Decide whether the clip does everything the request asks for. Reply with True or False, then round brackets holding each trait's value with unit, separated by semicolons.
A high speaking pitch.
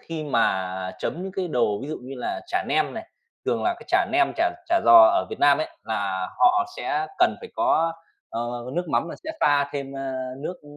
False (155 Hz)